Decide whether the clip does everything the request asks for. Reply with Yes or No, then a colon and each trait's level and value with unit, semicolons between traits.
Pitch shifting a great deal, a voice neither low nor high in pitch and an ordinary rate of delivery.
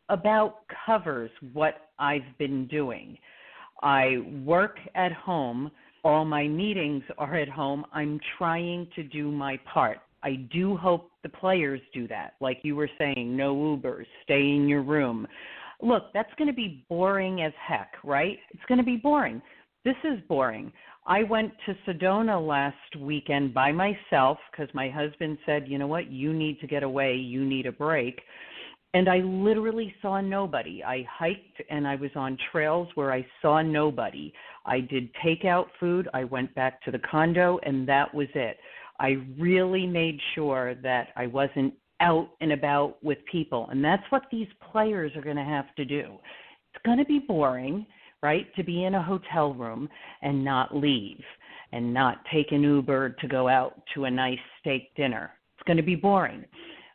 No: average, 4.9 semitones; medium, 150 Hz; average, 175 wpm